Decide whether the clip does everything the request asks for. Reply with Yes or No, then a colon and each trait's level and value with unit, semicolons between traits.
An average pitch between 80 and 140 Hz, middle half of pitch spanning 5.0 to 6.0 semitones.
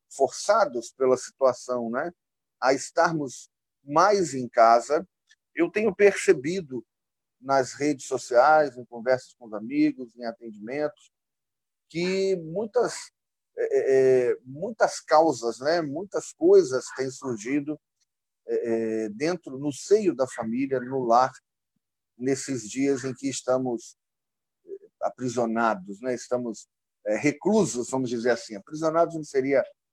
Yes: low, 135 Hz; average, 5.3 semitones